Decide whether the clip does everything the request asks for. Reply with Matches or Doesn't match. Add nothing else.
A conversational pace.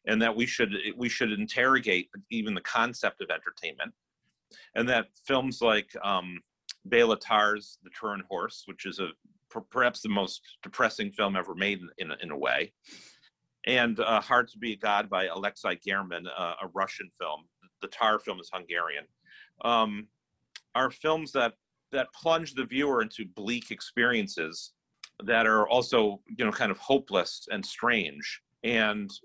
Matches